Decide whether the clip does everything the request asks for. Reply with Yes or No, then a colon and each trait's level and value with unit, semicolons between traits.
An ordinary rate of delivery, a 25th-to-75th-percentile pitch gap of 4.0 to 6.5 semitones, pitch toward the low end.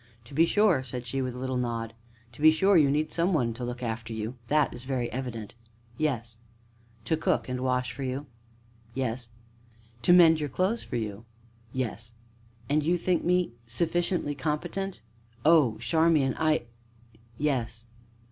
Yes: average, 165 wpm; average, 5.1 semitones; low, 130 Hz